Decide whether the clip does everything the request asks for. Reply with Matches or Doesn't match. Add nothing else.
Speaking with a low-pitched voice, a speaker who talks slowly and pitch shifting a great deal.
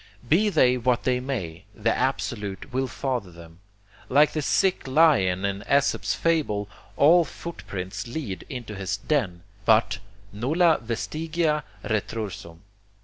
Matches